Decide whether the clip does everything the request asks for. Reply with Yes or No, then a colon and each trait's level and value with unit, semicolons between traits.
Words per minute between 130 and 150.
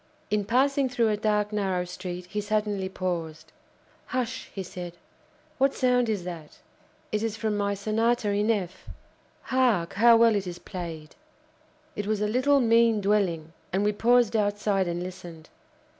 No: average, 160 wpm